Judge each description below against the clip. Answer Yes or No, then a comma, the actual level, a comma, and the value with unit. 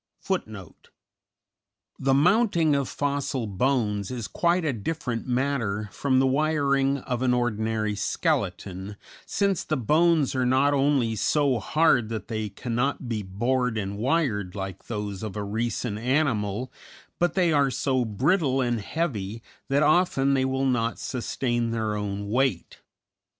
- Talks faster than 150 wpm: No, average, 140 wpm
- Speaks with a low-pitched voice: Yes, low, 125 Hz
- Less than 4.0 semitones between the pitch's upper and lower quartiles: No, average, 4.7 semitones